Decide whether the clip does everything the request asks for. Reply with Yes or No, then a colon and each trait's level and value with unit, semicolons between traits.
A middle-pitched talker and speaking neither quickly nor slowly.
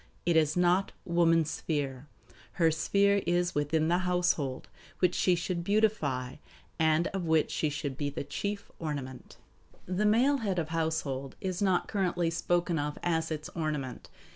Yes: medium, 165 Hz; average, 160 wpm